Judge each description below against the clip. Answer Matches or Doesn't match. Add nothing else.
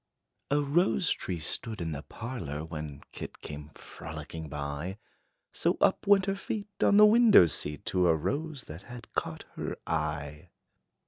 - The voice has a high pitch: Doesn't match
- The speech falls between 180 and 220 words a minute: Doesn't match